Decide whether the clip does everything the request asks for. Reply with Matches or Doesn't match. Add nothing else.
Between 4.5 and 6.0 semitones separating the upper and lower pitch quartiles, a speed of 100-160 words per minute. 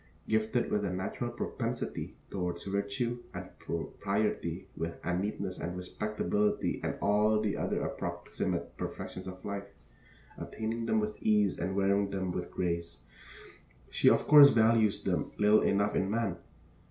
Doesn't match